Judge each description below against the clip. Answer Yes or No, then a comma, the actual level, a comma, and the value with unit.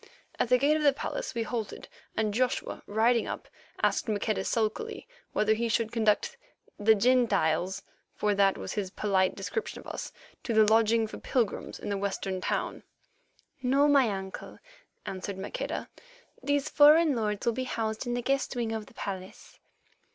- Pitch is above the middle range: Yes, high, 220 Hz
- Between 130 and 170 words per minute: Yes, average, 165 wpm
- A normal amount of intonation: Yes, average, 3.7 semitones